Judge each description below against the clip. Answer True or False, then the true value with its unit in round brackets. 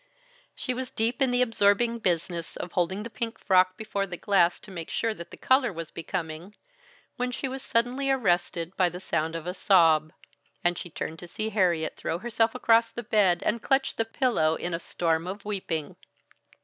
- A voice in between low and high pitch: False (195 Hz)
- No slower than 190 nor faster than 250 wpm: True (195 wpm)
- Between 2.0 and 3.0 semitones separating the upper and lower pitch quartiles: False (5.2 semitones)